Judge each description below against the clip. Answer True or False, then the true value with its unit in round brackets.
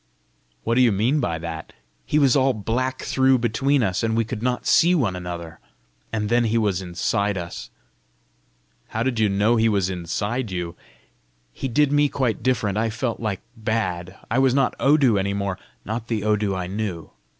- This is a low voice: True (110 Hz)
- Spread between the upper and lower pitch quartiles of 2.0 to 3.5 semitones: False (4.6 semitones)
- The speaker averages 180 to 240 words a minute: True (185 wpm)